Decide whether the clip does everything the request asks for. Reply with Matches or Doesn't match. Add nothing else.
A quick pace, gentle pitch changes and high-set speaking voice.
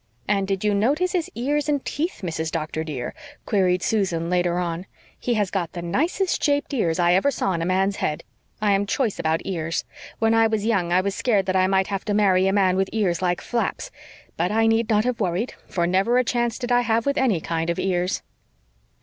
Doesn't match